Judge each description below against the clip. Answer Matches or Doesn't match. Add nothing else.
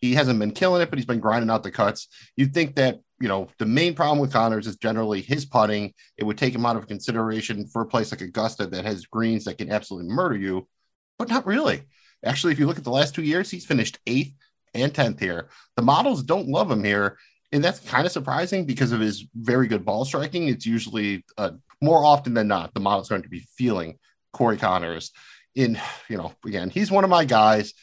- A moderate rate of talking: Doesn't match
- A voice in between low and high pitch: Doesn't match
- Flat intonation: Doesn't match